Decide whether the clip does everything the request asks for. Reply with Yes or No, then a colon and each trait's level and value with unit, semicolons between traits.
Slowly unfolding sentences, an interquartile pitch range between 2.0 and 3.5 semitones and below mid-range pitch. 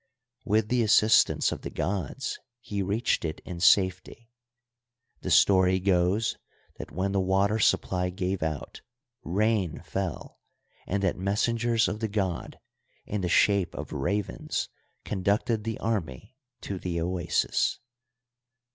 Yes: slow, 130 wpm; average, 2.8 semitones; low, 100 Hz